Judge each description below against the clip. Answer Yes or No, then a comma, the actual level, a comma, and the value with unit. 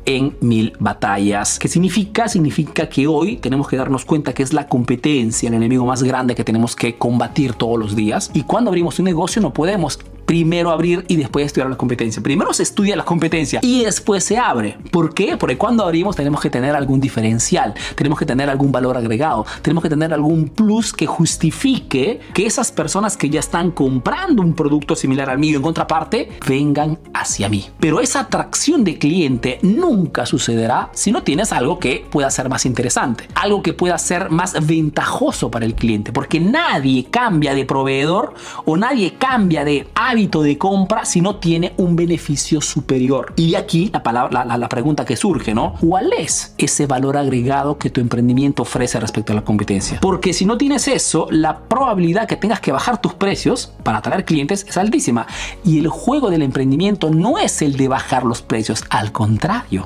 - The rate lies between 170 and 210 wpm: Yes, fast, 190 wpm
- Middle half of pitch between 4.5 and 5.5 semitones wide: Yes, average, 5.2 semitones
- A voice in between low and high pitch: Yes, medium, 150 Hz